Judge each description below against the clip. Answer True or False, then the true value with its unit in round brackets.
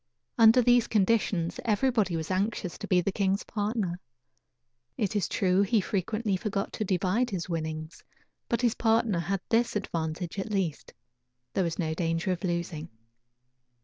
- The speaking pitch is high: True (195 Hz)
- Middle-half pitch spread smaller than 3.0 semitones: False (4.2 semitones)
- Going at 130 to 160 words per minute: True (150 wpm)